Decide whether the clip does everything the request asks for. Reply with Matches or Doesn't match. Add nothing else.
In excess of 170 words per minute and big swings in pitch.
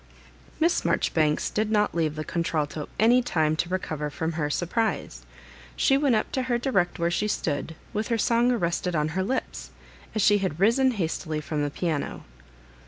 Matches